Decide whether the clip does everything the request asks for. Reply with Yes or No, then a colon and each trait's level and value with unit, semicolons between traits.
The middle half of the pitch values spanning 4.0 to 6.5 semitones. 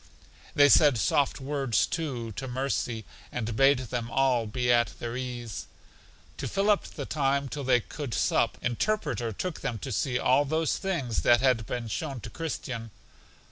No: average, 3.2 semitones